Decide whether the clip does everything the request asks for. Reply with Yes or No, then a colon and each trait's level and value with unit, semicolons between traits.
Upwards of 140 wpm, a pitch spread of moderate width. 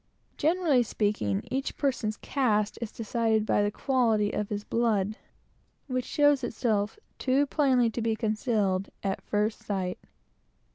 No: slow, 135 wpm; average, 3.6 semitones